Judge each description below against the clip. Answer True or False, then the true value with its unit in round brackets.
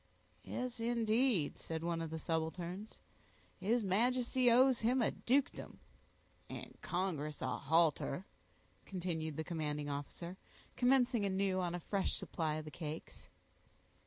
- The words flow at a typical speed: False (130 wpm)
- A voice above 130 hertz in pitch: True (185 Hz)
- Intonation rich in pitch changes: True (6.5 semitones)